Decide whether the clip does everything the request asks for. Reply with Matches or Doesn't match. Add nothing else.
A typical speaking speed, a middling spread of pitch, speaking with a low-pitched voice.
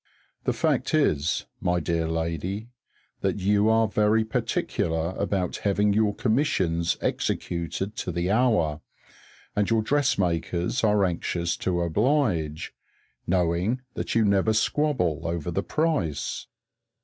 Doesn't match